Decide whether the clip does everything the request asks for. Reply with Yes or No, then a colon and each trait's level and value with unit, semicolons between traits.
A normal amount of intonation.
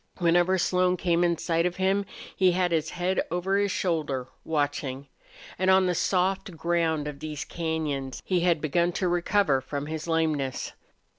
Yes: average, 3.0 semitones